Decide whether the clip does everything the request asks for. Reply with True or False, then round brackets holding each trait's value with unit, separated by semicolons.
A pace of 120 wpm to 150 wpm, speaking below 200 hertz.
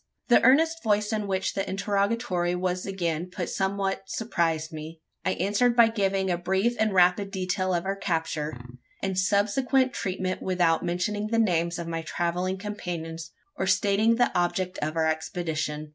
False (160 wpm; 185 Hz)